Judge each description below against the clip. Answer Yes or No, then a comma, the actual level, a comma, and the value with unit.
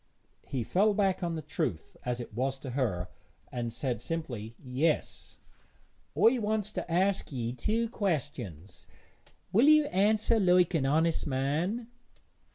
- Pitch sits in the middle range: Yes, medium, 160 Hz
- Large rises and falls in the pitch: Yes, wide, 8.1 semitones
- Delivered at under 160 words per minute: Yes, average, 140 wpm